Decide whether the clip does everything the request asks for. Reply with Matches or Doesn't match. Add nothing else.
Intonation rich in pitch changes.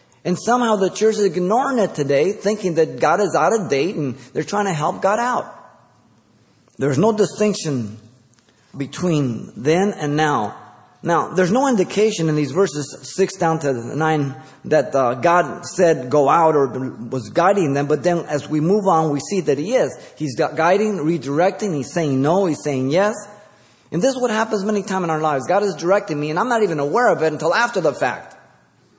Matches